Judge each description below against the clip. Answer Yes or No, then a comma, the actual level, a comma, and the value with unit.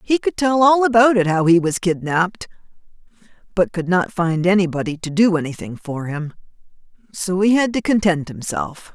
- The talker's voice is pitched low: No, medium, 185 Hz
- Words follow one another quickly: No, average, 170 wpm